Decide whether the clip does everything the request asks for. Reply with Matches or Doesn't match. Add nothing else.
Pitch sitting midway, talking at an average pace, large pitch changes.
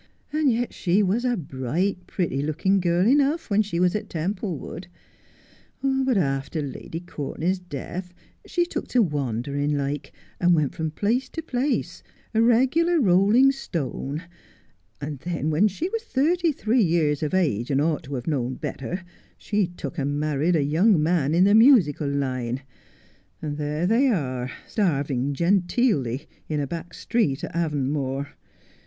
Matches